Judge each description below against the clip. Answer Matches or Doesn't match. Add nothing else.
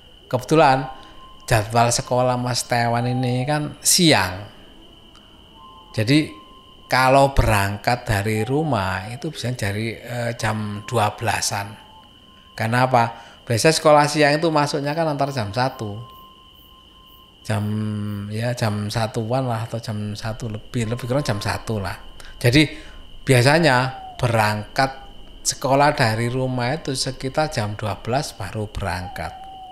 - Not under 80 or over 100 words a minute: Doesn't match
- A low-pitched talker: Matches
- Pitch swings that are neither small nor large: Matches